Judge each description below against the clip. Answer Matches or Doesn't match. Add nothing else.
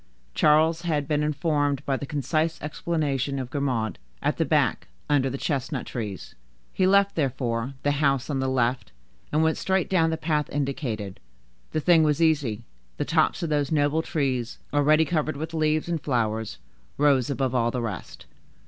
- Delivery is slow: Doesn't match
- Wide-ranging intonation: Doesn't match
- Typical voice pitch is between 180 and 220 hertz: Doesn't match